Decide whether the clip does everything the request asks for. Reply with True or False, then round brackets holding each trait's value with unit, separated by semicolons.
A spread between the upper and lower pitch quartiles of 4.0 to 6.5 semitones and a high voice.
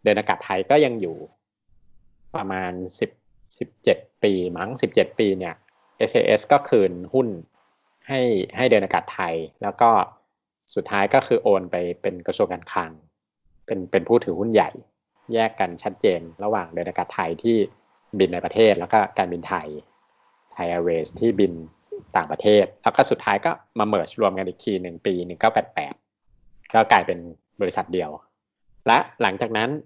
False (4.7 semitones; 95 Hz)